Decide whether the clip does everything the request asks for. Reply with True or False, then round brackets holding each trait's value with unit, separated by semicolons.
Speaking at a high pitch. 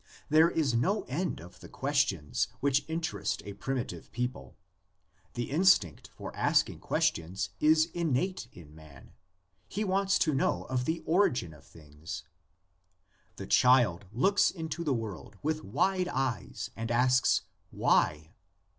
False (125 Hz)